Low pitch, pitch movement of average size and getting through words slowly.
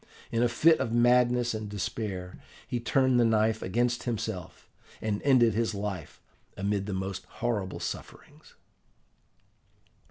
Yes: low, 110 Hz; average, 3.2 semitones; slow, 130 wpm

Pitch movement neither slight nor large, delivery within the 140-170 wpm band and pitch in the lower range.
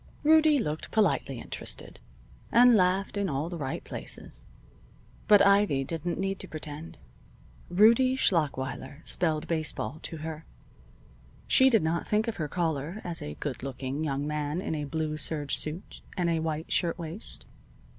No: average, 4.6 semitones; average, 150 wpm; medium, 160 Hz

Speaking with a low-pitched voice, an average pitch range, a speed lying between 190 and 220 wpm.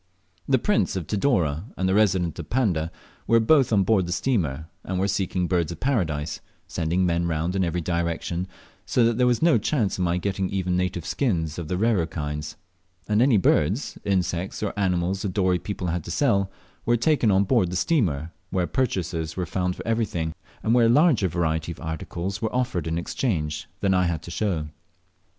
Yes: very low, 90 Hz; average, 4.2 semitones; average, 195 wpm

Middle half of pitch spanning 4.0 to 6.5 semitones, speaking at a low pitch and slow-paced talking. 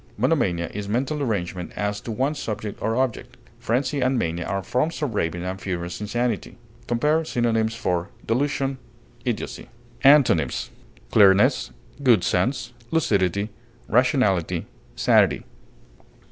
Yes: wide, 5.5 semitones; low, 110 Hz; slow, 120 wpm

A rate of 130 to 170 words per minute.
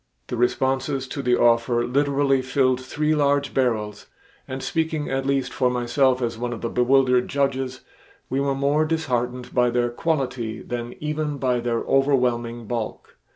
Yes: average, 155 wpm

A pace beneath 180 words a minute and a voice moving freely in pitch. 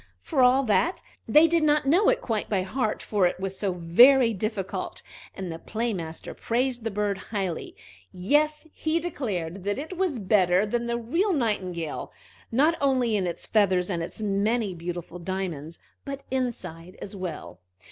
Yes: average, 165 wpm; wide, 6.3 semitones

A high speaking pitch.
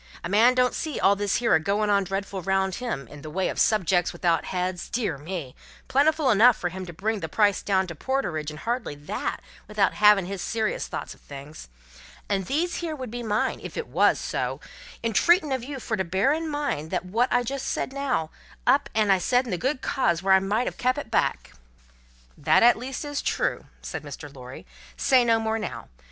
Yes: high, 210 Hz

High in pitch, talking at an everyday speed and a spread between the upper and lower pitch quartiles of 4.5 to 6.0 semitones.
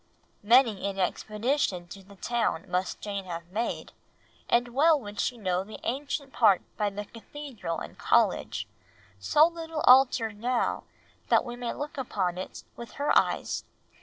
Yes: high, 225 Hz; average, 155 wpm; average, 5.2 semitones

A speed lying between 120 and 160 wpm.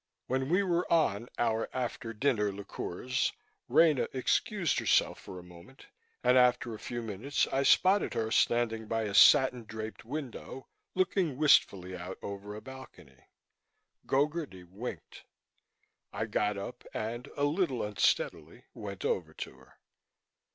Yes: slow, 135 wpm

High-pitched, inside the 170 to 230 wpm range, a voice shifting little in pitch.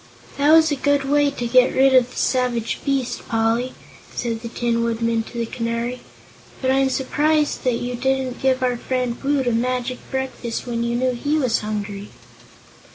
Yes: very high, 250 Hz; average, 180 wpm; narrow, 2.2 semitones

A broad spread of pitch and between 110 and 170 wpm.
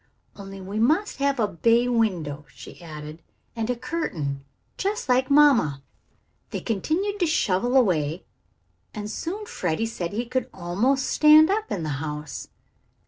Yes: wide, 8.7 semitones; average, 145 wpm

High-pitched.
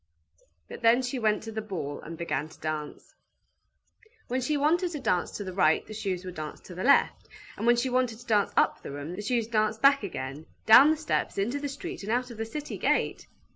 Yes: high, 220 Hz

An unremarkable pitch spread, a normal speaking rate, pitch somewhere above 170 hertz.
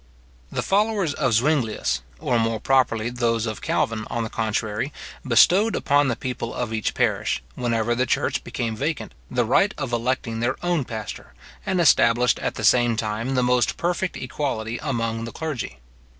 No: average, 3.4 semitones; average, 165 wpm; low, 120 Hz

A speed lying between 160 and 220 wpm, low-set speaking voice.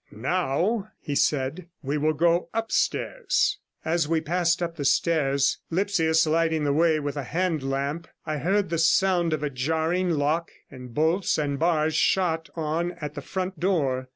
No: average, 165 wpm; medium, 160 Hz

